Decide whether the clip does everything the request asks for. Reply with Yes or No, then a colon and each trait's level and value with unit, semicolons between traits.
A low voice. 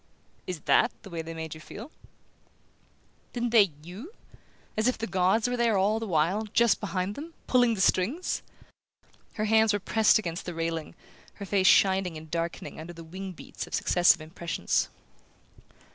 No: high, 190 Hz